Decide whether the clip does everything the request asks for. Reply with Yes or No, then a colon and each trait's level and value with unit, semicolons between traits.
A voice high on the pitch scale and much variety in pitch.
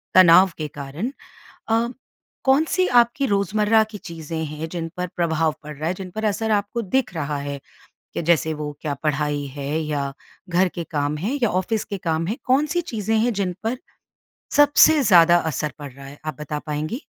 No: medium, 175 Hz; wide, 6.5 semitones